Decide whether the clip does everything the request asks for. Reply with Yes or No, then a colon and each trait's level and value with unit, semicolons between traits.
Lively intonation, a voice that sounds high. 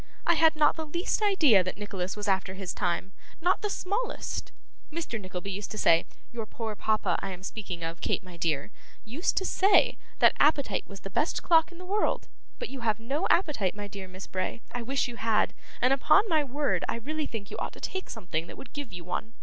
Yes: wide, 8.5 semitones; high, 225 Hz